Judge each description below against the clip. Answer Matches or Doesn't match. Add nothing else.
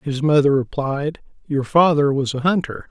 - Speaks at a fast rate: Doesn't match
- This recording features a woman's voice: Doesn't match